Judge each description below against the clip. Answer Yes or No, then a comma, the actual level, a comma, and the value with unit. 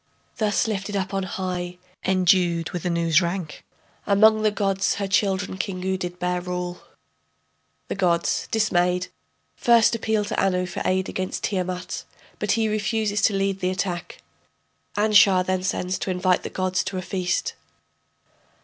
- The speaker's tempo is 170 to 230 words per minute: No, average, 150 wpm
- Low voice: No, medium, 185 Hz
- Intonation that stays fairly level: Yes, narrow, 2.0 semitones